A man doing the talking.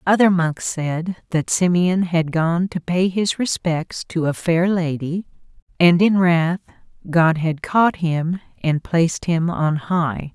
No: female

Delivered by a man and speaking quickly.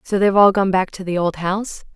No: female; fast, 275 wpm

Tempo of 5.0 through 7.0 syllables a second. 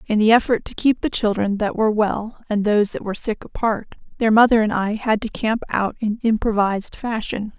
Yes: 5.4 syllables/s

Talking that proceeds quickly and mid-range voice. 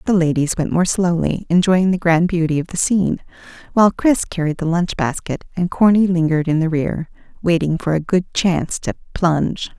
No: average, 190 wpm; medium, 170 Hz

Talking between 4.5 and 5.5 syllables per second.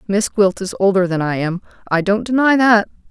Yes: 5.2 syllables/s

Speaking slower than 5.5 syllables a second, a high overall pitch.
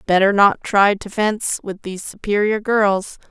Yes: 4.6 syllables/s; high, 200 Hz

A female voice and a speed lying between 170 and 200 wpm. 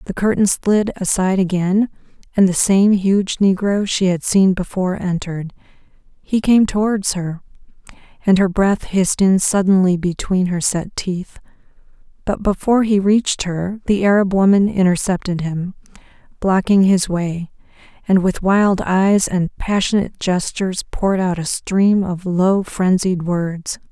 No: female; average, 145 wpm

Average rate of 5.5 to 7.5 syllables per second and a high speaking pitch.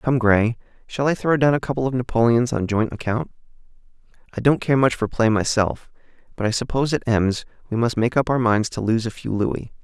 No: 5.6 syllables/s; low, 120 Hz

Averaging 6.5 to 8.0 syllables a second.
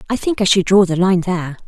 Yes: 6.6 syllables/s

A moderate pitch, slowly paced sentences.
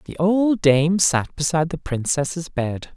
No: medium, 160 Hz; average, 160 wpm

